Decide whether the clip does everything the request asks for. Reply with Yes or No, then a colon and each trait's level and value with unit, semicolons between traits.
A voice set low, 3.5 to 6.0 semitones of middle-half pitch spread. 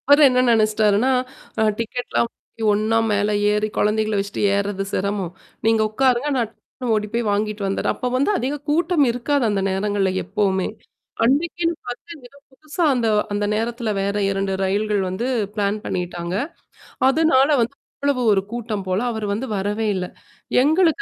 No: high, 215 Hz; average, 4.0 semitones